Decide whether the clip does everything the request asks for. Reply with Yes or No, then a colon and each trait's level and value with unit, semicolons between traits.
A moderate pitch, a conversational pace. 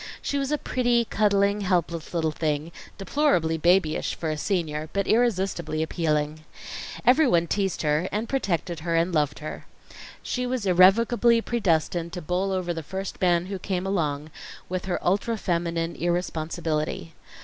Yes: medium, 180 Hz; average, 150 wpm